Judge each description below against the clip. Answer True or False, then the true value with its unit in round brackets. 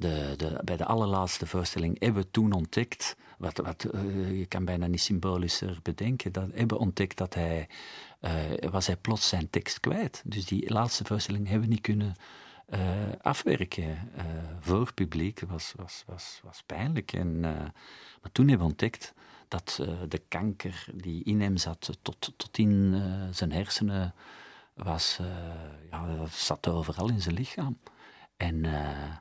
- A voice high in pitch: False (90 Hz)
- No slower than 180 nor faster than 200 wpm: False (165 wpm)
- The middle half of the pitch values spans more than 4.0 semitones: False (3.4 semitones)